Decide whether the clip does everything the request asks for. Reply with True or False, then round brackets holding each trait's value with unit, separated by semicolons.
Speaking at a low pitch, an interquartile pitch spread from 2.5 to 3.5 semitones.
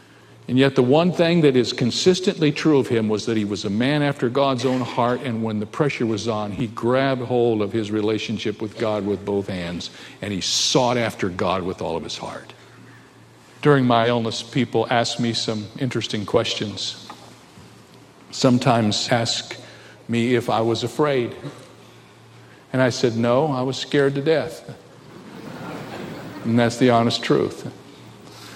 True (120 Hz; 2.8 semitones)